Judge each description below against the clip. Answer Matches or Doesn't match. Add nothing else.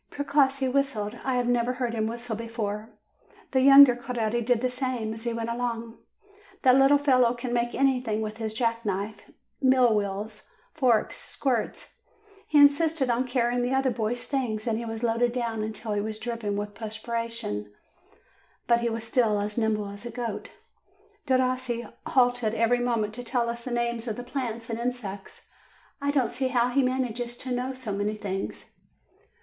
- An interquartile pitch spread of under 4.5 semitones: Matches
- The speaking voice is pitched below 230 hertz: Doesn't match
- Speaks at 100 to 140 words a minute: Doesn't match